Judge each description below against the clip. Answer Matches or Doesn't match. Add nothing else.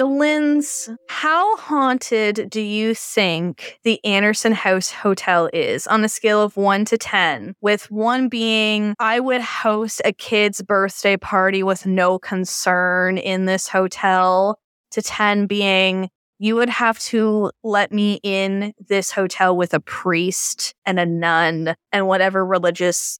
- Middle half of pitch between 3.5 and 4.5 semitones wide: Doesn't match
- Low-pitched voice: Doesn't match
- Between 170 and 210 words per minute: Doesn't match